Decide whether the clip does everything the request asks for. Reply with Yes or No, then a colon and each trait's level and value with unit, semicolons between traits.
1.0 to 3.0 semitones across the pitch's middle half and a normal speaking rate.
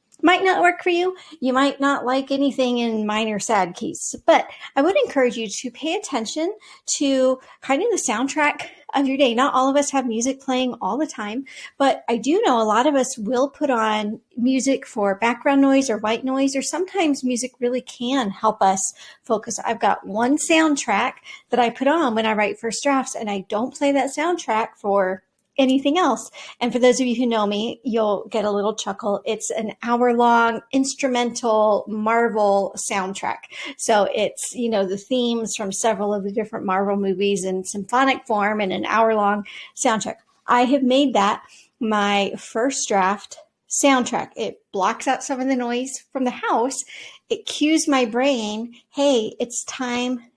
No: average, 4.0 semitones; average, 185 wpm